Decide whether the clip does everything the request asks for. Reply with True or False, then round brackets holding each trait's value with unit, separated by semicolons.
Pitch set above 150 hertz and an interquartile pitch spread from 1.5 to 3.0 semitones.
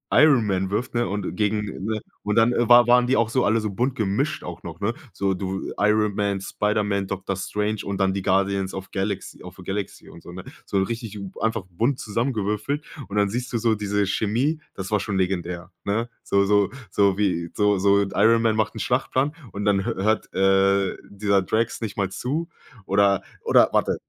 False (105 Hz; 2.7 semitones)